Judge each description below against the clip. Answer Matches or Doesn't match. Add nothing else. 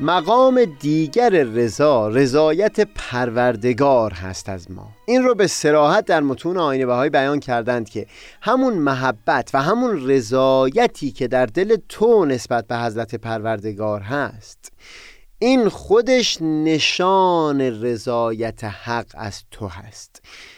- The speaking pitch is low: Matches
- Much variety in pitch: Matches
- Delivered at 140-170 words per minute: Doesn't match